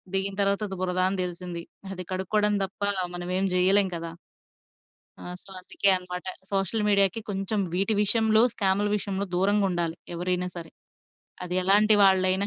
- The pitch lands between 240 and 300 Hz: No, high, 190 Hz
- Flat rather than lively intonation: Yes, narrow, 1.8 semitones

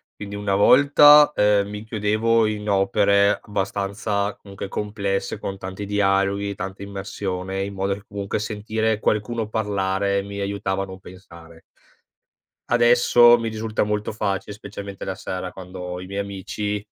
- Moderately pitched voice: No, low, 100 Hz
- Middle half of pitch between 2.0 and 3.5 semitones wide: No, narrow, 1.5 semitones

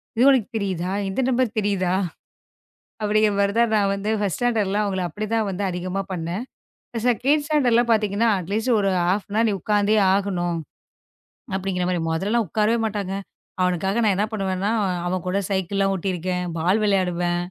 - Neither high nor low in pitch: No, high, 200 Hz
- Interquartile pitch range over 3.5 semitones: No, average, 2.9 semitones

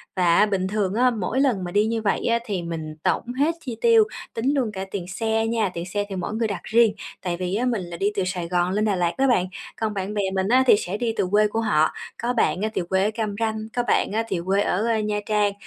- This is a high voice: Yes, high, 210 Hz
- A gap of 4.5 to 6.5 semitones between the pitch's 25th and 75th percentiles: No, average, 3.4 semitones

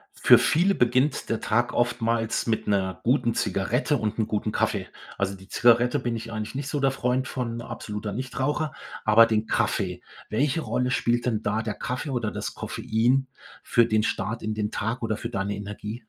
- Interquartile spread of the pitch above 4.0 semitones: No, average, 2.8 semitones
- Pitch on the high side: No, low, 115 Hz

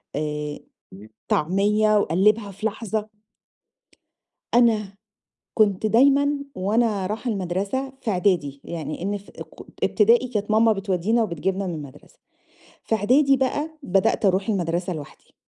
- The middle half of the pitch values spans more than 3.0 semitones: Yes, average, 3.6 semitones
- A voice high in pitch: Yes, high, 205 Hz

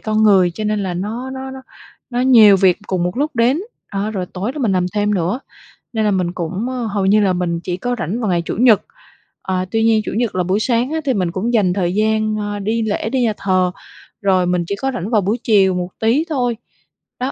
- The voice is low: No, high, 210 Hz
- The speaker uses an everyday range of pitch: Yes, average, 4.1 semitones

